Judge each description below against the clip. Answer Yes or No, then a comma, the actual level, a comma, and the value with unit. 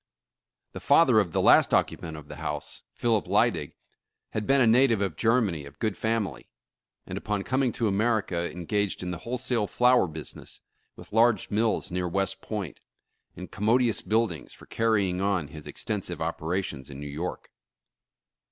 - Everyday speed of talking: Yes, average, 160 wpm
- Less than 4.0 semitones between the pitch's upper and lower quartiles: No, average, 4.5 semitones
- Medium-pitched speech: No, low, 100 Hz